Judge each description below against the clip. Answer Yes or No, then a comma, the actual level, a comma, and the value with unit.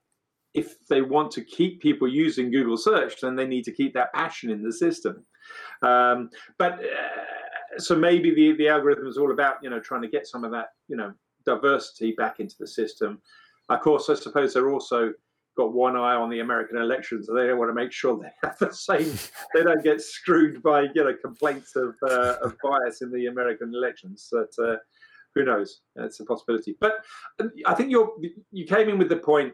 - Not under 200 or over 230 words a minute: Yes, fast, 205 wpm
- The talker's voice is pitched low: No, medium, 165 Hz